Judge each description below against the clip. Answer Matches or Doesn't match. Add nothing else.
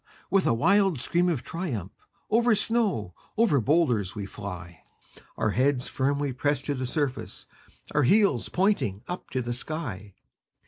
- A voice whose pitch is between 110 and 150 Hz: Matches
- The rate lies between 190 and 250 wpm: Doesn't match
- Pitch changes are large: Matches